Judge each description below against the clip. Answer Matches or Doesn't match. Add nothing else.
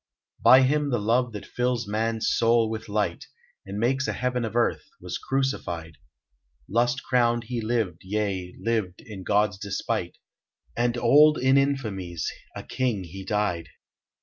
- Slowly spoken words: Doesn't match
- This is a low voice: Matches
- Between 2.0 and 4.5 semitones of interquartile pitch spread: Matches